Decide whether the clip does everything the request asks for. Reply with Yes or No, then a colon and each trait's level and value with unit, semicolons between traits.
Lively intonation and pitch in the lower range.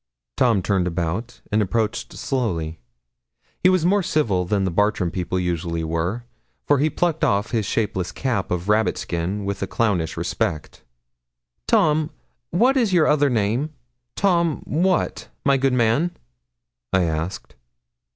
Yes: wide, 8.5 semitones; low, 110 Hz